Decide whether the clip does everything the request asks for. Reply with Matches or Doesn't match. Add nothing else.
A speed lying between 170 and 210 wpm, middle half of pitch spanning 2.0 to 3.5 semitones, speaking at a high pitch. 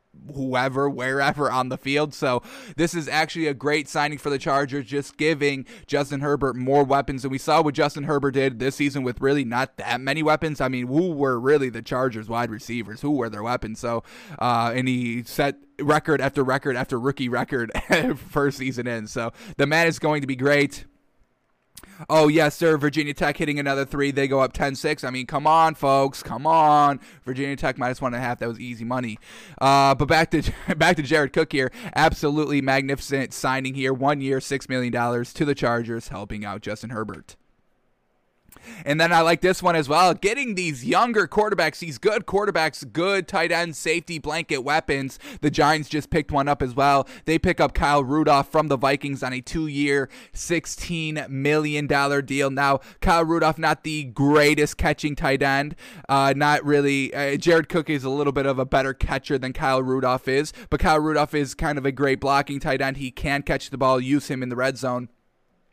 Doesn't match